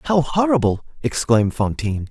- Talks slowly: Yes, slow, 115 wpm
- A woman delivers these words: No, male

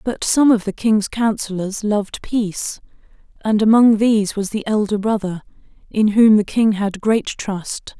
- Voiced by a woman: Yes, female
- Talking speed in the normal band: Yes, average, 165 wpm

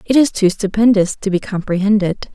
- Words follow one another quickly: No, average, 180 wpm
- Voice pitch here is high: Yes, high, 200 Hz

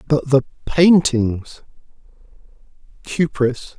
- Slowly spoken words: Yes, slow, 50 wpm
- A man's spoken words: Yes, male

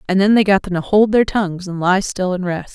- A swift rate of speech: Yes, fast, 305 wpm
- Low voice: No, high, 190 Hz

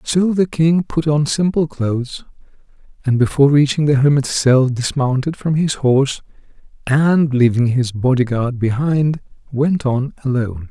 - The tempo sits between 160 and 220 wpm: No, average, 145 wpm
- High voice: No, medium, 140 Hz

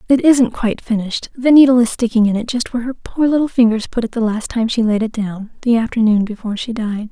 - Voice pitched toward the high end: Yes, high, 230 Hz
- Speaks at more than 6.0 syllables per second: Yes, 6.2 syllables/s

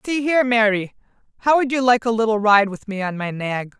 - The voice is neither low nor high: No, high, 225 Hz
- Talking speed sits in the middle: No, fast, 235 wpm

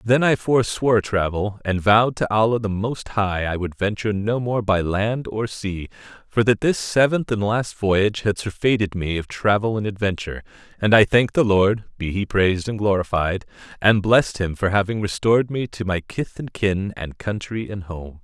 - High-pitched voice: No, low, 105 Hz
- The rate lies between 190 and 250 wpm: Yes, average, 195 wpm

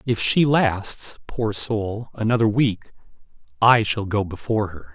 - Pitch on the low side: Yes, low, 110 Hz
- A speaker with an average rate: Yes, average, 145 wpm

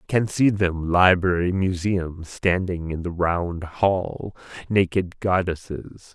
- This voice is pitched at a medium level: No, very low, 90 Hz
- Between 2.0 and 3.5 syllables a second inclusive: Yes, 3.4 syllables/s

